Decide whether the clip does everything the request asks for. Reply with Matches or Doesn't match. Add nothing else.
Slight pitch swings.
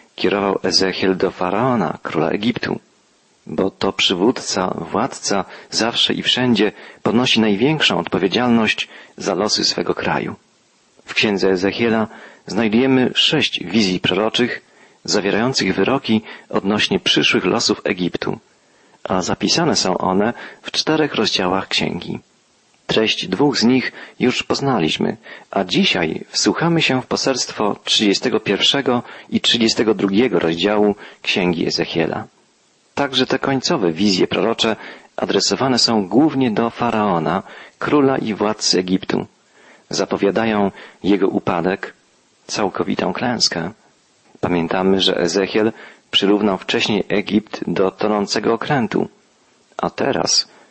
Doesn't match